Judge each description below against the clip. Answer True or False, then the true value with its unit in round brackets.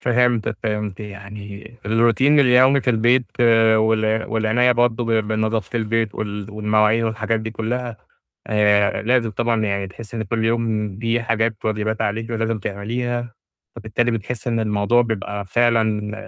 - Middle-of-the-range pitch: False (110 Hz)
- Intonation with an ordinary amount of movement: False (1.8 semitones)